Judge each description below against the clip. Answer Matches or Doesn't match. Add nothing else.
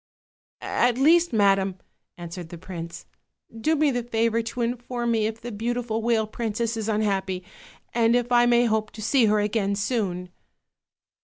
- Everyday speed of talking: Matches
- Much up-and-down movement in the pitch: Doesn't match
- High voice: Matches